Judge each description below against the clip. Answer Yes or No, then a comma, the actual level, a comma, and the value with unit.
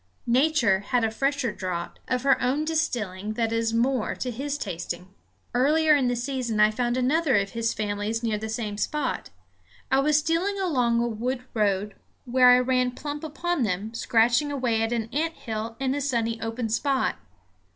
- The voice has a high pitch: Yes, high, 245 Hz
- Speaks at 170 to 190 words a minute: Yes, average, 180 wpm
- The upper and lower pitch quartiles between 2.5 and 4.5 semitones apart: Yes, average, 3.7 semitones